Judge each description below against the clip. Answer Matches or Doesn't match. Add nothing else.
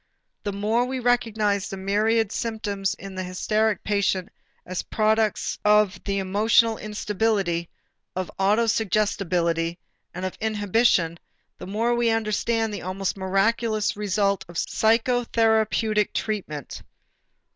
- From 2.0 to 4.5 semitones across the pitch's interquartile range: Matches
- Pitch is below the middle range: Doesn't match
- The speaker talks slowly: Matches